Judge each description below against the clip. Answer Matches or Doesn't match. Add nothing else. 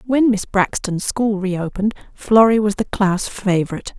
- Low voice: Doesn't match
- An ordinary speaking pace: Matches